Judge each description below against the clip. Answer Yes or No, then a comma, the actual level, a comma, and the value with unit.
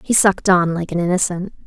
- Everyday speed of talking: No, fast, 215 wpm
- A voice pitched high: No, medium, 180 Hz